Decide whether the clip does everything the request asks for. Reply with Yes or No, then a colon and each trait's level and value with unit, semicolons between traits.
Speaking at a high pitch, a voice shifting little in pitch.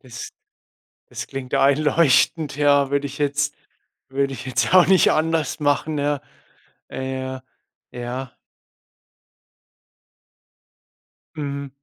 No: medium, 140 Hz; narrow, 2.0 semitones